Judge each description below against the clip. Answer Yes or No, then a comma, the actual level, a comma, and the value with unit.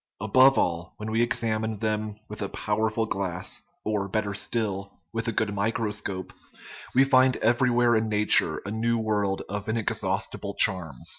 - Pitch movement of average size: No, narrow, 2.2 semitones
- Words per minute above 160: No, average, 155 wpm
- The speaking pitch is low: Yes, low, 110 Hz